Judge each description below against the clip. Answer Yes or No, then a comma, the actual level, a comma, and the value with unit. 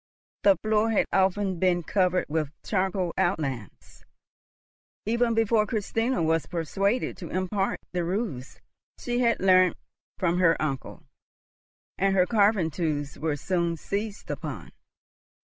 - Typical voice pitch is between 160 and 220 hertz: Yes, medium, 185 Hz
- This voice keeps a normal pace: No, slow, 125 wpm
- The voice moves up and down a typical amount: Yes, average, 3.8 semitones